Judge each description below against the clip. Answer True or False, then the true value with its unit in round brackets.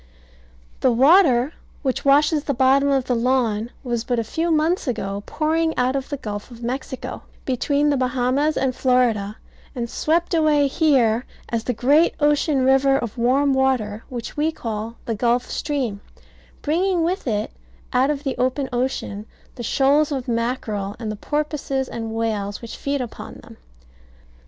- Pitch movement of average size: True (3.7 semitones)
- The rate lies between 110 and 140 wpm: False (160 wpm)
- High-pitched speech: True (260 Hz)